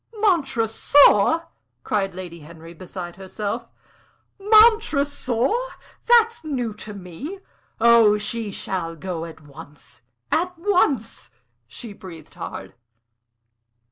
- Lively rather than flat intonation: Yes, wide, 9.0 semitones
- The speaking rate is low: Yes, slow, 95 wpm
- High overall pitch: Yes, high, 220 Hz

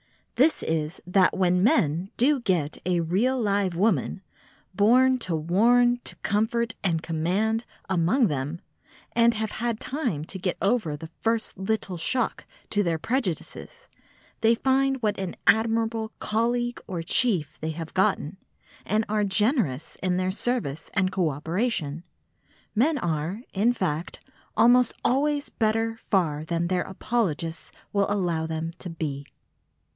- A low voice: No, high, 200 Hz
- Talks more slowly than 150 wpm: Yes, average, 140 wpm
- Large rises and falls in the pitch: Yes, wide, 5.7 semitones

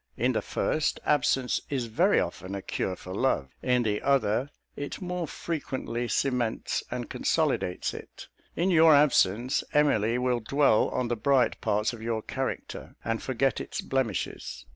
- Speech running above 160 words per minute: No, average, 155 wpm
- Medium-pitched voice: No, low, 125 Hz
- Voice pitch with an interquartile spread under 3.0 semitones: No, average, 4.3 semitones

